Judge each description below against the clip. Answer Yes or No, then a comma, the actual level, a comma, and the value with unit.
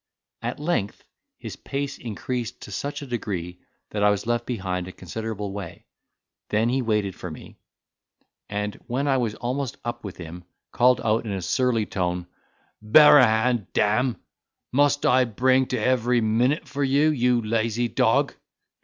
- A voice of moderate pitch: No, low, 115 Hz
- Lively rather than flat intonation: No, average, 3.7 semitones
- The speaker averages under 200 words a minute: Yes, average, 160 wpm